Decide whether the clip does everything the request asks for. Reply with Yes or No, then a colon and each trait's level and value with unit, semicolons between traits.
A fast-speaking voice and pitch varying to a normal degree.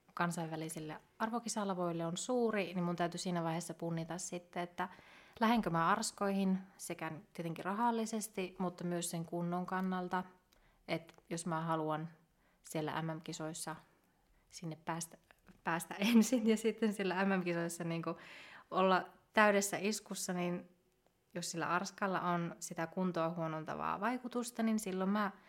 No: average, 125 wpm; average, 3.1 semitones